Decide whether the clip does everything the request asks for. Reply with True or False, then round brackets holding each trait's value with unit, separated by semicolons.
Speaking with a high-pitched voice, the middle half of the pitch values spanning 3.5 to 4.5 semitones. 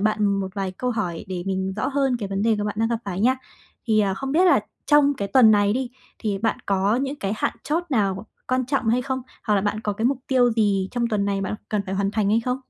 True (215 Hz; 4.0 semitones)